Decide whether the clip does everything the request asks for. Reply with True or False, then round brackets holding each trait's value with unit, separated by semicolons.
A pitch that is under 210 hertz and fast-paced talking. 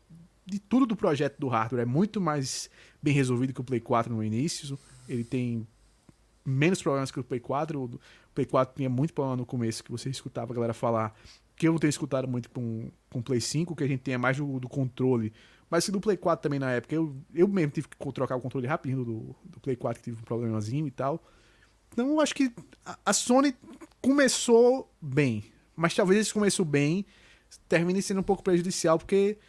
True (140 Hz; 215 wpm)